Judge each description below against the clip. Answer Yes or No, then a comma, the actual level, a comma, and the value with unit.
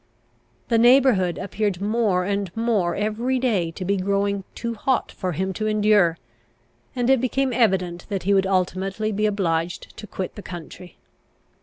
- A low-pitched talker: No, high, 200 Hz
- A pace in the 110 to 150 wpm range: No, average, 160 wpm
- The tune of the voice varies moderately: Yes, average, 3.4 semitones